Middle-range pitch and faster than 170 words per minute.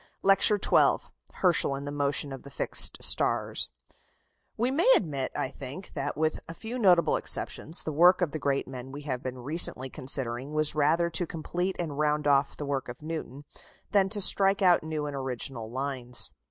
Yes: medium, 150 Hz; average, 185 wpm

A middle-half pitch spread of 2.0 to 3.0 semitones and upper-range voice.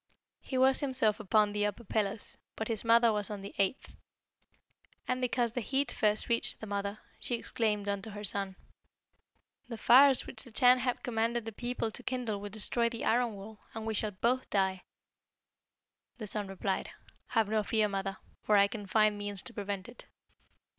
Yes: average, 2.7 semitones; high, 220 Hz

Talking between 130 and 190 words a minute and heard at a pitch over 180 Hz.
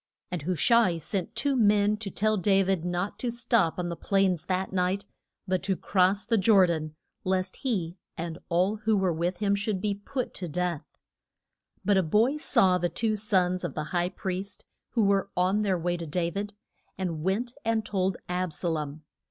No: average, 200 wpm; high, 190 Hz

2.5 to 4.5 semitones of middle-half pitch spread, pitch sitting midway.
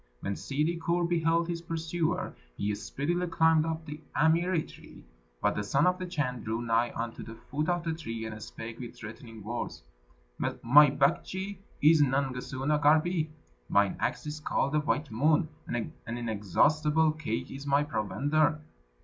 No: wide, 5.5 semitones; medium, 150 Hz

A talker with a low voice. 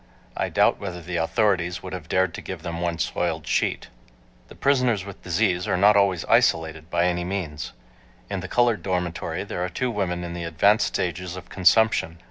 Yes: very low, 90 Hz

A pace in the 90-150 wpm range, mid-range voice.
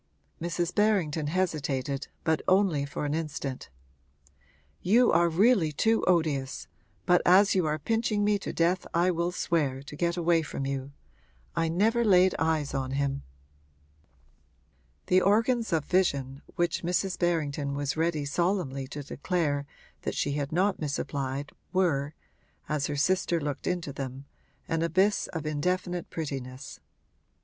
Yes: average, 140 wpm; medium, 165 Hz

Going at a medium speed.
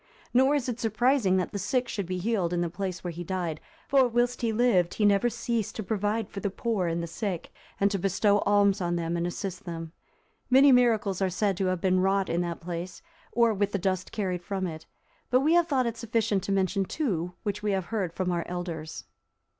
No: fast, 225 wpm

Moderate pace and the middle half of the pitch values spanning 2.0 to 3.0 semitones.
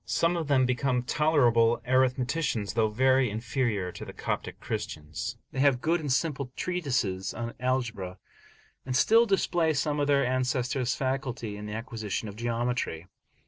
No: average, 150 wpm; average, 3.6 semitones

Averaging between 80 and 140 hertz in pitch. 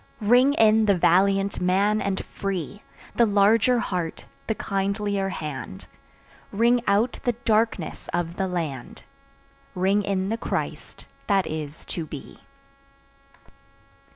No: high, 195 Hz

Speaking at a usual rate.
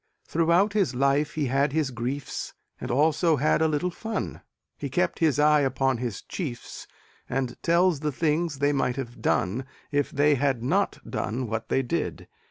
Yes: average, 175 wpm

